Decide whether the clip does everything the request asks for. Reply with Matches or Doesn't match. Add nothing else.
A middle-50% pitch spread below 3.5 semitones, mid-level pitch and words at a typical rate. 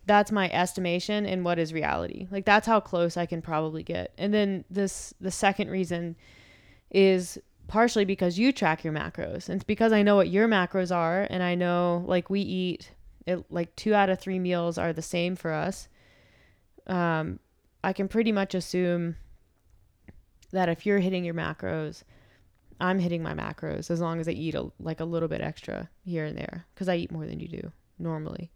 Matches